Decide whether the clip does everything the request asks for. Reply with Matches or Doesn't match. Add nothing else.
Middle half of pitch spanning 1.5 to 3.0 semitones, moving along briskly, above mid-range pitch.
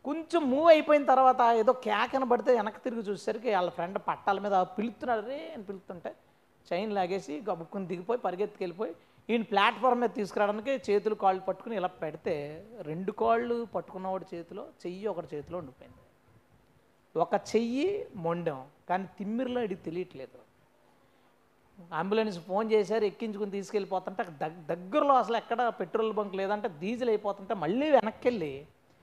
Doesn't match